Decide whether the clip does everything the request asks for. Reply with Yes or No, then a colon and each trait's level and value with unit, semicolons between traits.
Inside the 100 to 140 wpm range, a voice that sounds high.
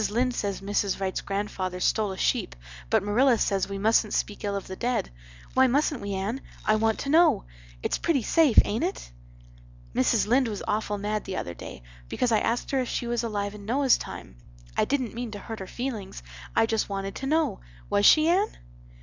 No: fast, 205 wpm; high, 215 Hz